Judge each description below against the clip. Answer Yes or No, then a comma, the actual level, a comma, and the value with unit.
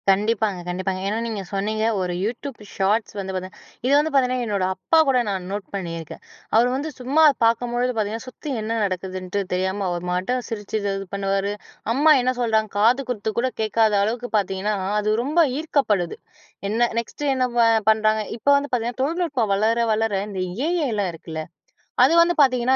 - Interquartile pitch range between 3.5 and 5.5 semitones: Yes, average, 4.3 semitones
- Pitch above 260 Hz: No, high, 220 Hz